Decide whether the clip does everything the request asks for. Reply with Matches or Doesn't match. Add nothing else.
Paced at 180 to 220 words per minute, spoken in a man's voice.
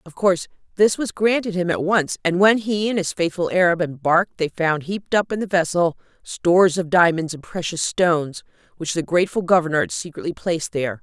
Doesn't match